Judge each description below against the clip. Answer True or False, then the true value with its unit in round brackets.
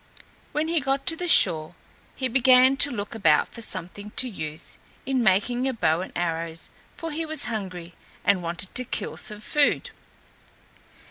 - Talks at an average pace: True (165 wpm)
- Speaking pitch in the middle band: False (215 Hz)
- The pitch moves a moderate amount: False (7.3 semitones)